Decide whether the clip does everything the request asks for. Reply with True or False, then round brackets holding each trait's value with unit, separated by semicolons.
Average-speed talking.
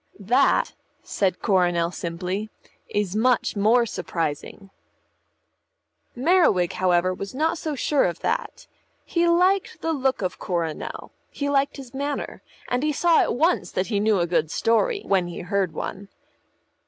True (145 wpm)